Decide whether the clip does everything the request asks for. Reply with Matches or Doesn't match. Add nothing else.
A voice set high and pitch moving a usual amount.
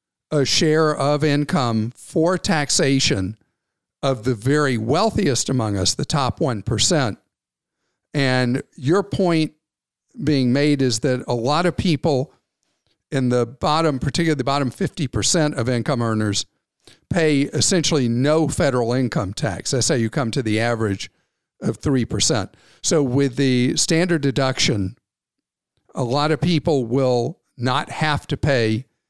Doesn't match